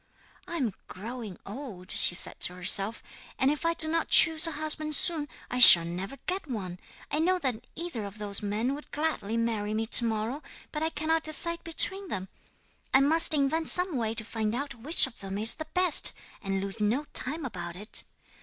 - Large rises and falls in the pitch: Yes, wide, 7.0 semitones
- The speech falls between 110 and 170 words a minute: No, average, 200 wpm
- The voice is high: Yes, very high, 250 Hz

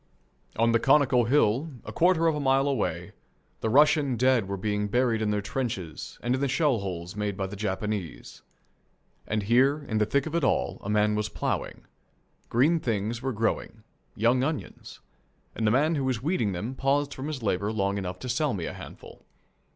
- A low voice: Yes, low, 115 Hz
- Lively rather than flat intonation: No, average, 4.7 semitones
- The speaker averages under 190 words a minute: No, average, 195 wpm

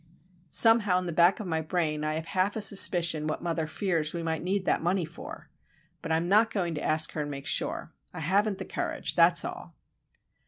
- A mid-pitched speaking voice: Yes, medium, 170 Hz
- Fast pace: Yes, fast, 220 wpm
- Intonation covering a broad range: No, average, 3.3 semitones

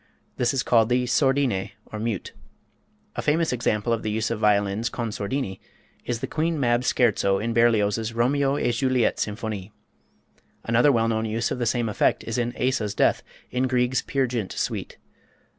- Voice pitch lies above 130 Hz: No, low, 115 Hz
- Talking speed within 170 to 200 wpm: Yes, average, 175 wpm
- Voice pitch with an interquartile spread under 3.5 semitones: Yes, narrow, 2.6 semitones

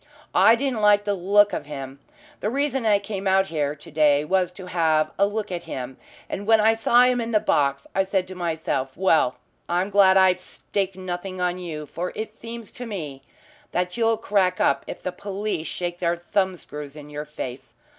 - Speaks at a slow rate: No, fast, 205 wpm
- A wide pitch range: No, average, 4.7 semitones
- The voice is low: No, medium, 185 Hz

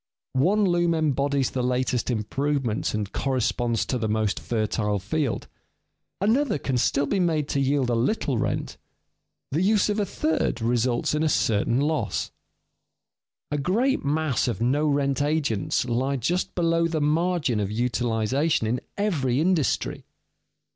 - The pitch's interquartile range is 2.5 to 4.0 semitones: No, average, 5.0 semitones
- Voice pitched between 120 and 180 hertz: Yes, medium, 140 Hz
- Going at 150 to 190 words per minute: No, average, 140 wpm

